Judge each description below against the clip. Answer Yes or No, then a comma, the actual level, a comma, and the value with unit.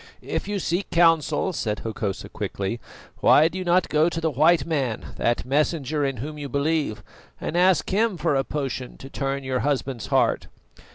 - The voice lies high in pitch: No, medium, 145 Hz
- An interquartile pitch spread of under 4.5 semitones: Yes, average, 4.1 semitones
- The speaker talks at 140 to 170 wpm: No, average, 180 wpm